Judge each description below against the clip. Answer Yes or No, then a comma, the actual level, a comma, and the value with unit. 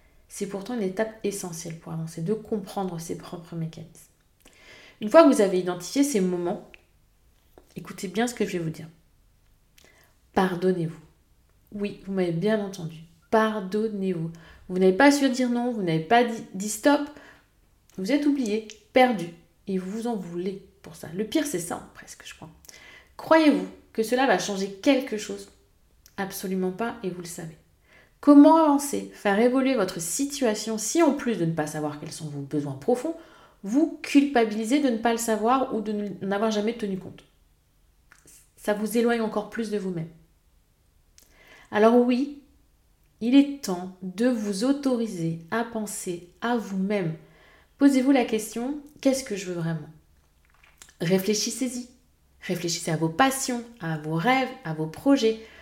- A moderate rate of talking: Yes, average, 160 wpm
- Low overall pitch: No, high, 205 Hz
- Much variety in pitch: Yes, wide, 6.1 semitones